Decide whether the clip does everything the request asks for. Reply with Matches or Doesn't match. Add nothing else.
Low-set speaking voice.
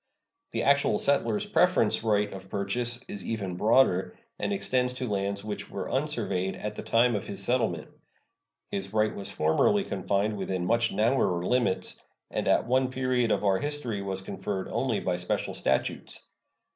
Matches